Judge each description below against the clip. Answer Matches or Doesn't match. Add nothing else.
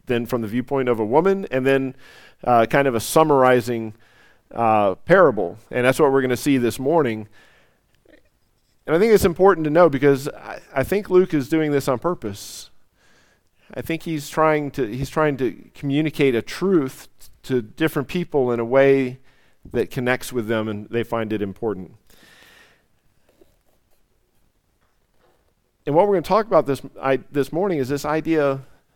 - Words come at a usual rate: Matches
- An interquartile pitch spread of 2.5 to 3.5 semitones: Doesn't match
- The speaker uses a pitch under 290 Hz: Matches